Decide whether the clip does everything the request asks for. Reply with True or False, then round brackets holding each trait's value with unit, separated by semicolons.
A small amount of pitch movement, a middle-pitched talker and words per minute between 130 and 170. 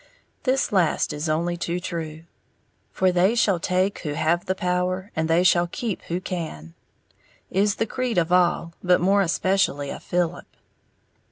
True (2.2 semitones; 180 Hz; 160 wpm)